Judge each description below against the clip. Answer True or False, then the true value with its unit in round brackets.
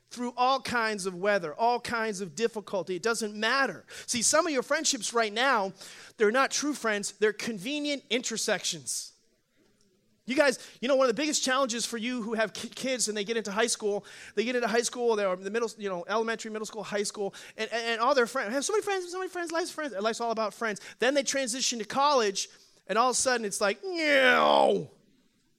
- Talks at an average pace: False (220 wpm)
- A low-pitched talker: False (230 Hz)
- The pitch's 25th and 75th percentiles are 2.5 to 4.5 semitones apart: True (3.9 semitones)